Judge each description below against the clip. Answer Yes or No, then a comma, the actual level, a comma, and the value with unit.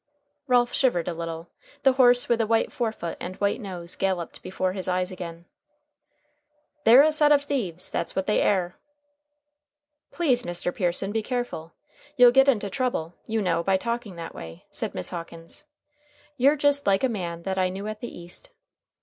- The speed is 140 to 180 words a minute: Yes, average, 175 wpm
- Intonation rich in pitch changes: Yes, wide, 5.8 semitones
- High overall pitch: Yes, high, 195 Hz